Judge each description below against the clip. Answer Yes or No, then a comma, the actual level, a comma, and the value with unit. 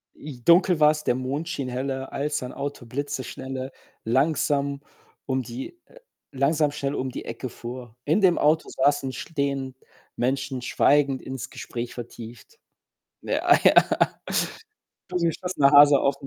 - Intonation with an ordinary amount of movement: No, narrow, 2.3 semitones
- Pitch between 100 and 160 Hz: Yes, medium, 140 Hz